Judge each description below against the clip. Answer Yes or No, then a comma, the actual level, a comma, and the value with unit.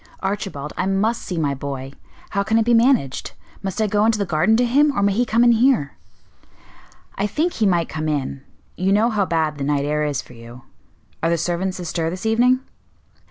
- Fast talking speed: Yes, fast, 210 wpm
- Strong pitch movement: Yes, wide, 6.7 semitones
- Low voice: No, high, 190 Hz